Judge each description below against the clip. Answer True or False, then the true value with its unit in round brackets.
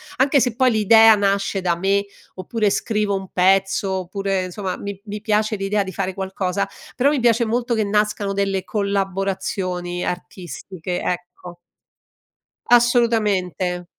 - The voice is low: False (195 Hz)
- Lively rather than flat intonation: False (2.5 semitones)